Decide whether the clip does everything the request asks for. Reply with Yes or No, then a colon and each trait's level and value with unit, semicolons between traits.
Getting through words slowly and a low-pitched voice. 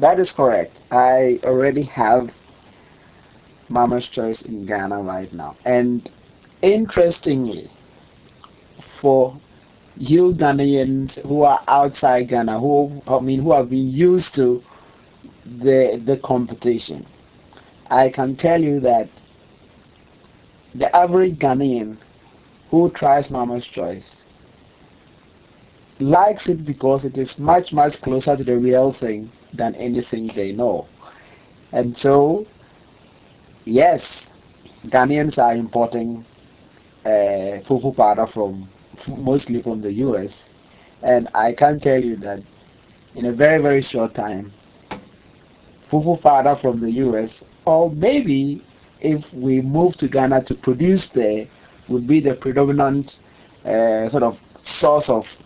Yes: slow, 120 wpm; low, 130 Hz